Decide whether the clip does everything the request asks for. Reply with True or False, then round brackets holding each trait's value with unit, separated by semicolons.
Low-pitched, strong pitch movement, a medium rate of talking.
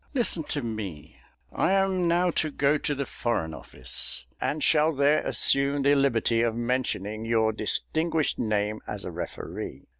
True (130 Hz; 6.0 semitones; 155 wpm)